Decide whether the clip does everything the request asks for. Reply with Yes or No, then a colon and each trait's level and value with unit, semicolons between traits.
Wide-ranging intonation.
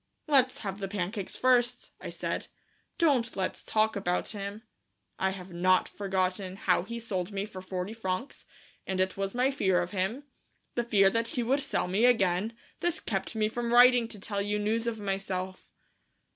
No: average, 3.6 semitones